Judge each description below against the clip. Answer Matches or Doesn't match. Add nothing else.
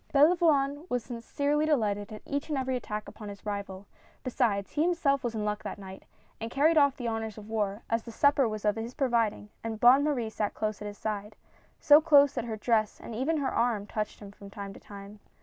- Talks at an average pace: Doesn't match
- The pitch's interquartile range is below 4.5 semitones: Doesn't match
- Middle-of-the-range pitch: Doesn't match